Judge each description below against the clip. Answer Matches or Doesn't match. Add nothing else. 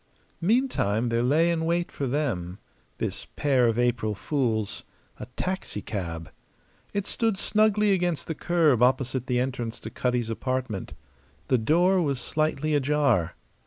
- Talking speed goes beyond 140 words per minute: Doesn't match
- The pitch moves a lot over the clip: Matches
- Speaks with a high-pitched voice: Doesn't match